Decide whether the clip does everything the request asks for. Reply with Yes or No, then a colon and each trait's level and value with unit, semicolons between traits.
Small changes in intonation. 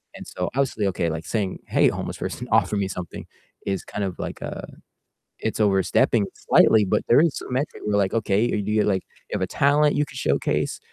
No: average, 3.7 semitones